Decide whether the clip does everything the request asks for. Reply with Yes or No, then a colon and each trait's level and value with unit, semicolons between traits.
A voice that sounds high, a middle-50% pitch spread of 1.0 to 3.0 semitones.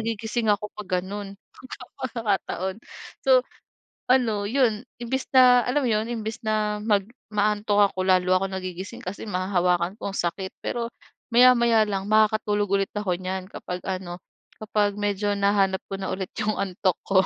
Yes: high, 205 Hz; narrow, 2.6 semitones